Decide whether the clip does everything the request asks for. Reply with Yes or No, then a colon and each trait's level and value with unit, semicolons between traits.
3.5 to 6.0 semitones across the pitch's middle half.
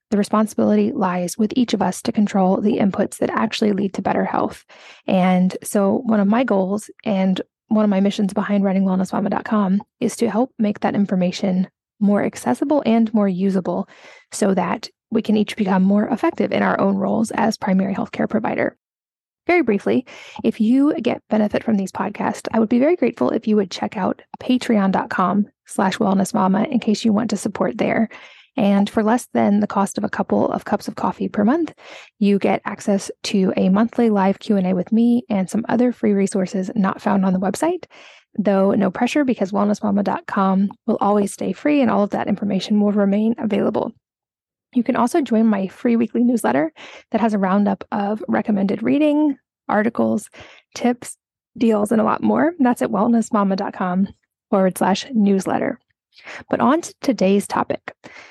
No: average, 2.8 semitones